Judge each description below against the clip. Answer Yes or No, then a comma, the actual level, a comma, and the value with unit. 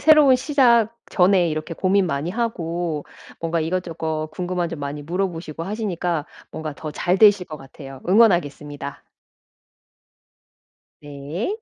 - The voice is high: No, medium, 170 Hz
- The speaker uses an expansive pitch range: No, average, 4.2 semitones